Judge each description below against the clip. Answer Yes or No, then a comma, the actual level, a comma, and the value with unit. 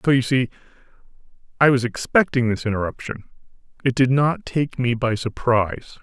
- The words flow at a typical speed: Yes, average, 150 wpm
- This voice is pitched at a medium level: No, low, 125 Hz